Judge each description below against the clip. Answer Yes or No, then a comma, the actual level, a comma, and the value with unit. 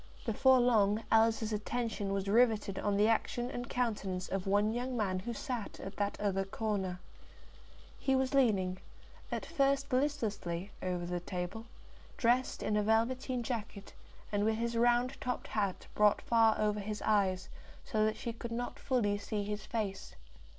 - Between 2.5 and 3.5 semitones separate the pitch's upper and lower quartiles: Yes, average, 3.2 semitones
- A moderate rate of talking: Yes, average, 160 wpm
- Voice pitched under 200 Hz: No, high, 215 Hz